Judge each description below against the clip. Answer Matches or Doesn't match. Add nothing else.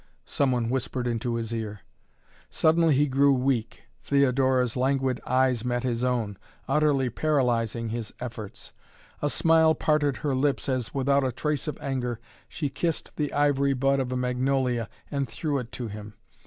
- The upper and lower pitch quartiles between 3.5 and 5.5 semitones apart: Doesn't match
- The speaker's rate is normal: Matches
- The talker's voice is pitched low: Matches